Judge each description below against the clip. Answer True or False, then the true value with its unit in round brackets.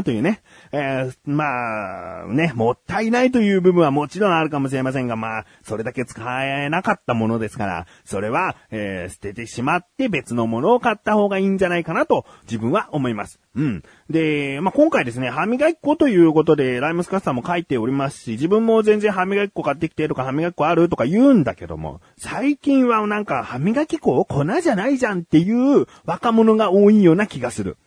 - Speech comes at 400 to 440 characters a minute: True (420 characters per minute)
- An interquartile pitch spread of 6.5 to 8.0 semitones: False (9.0 semitones)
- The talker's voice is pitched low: False (160 Hz)